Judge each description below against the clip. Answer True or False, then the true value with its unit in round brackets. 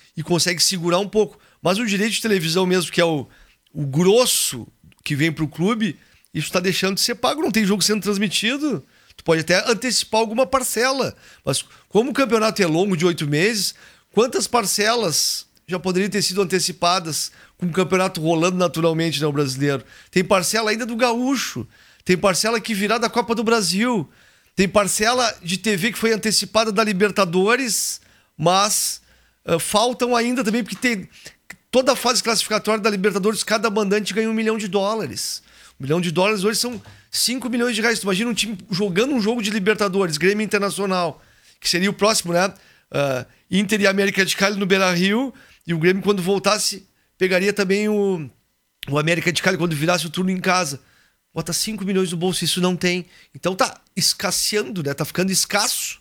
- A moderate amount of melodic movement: True (3.8 semitones)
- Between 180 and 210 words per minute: True (185 wpm)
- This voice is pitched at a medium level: False (195 Hz)